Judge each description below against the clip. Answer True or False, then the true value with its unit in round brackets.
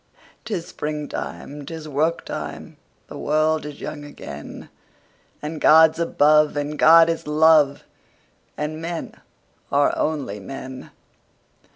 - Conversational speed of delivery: False (95 wpm)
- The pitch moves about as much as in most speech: False (1.6 semitones)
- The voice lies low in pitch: False (150 Hz)